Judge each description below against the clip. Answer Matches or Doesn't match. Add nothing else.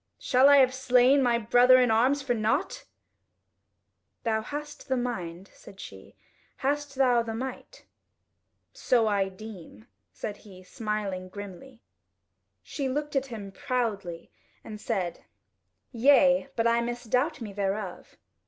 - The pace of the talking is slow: Matches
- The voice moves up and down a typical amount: Matches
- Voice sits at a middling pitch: Doesn't match